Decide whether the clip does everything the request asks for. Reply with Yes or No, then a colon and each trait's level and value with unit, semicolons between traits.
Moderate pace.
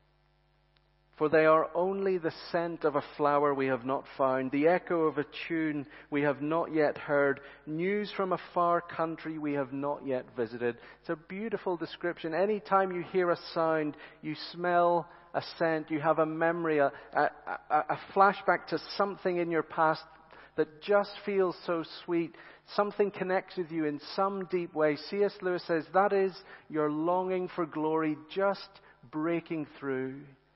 Yes: average, 165 wpm